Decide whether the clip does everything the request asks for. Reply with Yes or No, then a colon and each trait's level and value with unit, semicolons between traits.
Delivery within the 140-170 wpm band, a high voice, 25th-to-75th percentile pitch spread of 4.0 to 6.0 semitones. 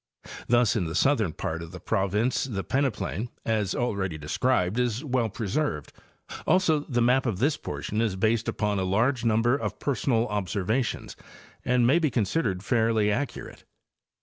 No: average, 155 wpm; low, 115 Hz; average, 4.3 semitones